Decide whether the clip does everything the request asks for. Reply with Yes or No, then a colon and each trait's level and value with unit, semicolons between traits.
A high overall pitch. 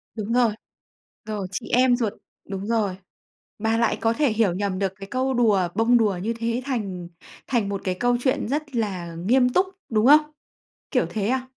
Yes: high, 225 Hz